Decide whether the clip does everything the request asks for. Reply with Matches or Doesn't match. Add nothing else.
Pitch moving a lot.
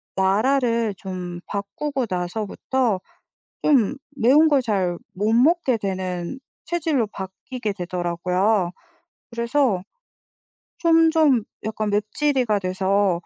Matches